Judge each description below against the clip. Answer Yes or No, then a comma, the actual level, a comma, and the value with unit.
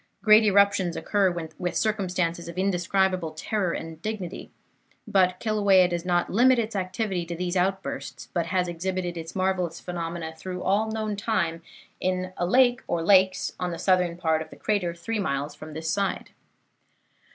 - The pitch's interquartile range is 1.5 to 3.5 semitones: Yes, average, 2.8 semitones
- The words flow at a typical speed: Yes, average, 165 wpm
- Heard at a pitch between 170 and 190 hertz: Yes, medium, 185 Hz